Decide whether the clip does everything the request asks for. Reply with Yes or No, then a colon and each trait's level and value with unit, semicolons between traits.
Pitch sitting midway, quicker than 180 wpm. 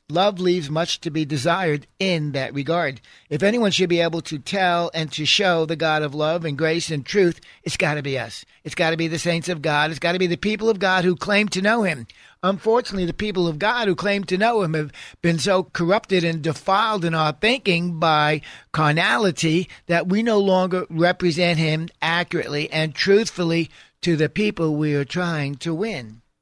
Yes: medium, 170 Hz; fast, 205 wpm